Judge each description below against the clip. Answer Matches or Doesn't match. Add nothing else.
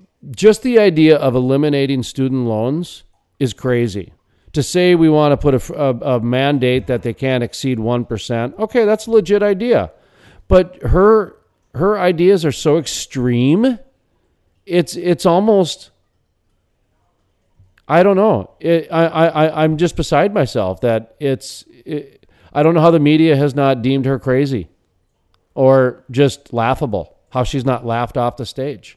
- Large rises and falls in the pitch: Matches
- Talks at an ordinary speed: Matches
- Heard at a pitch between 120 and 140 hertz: Matches